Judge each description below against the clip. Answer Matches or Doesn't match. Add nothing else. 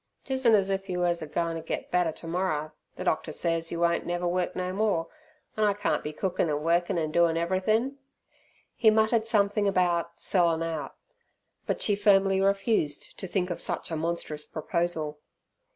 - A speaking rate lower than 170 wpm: Doesn't match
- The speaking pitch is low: Doesn't match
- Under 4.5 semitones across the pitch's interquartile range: Matches